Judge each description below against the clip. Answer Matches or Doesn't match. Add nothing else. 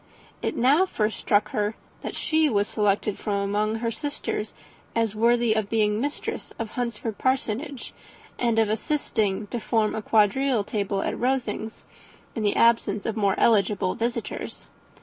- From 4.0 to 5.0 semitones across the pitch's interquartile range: Doesn't match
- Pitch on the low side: Doesn't match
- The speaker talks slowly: Doesn't match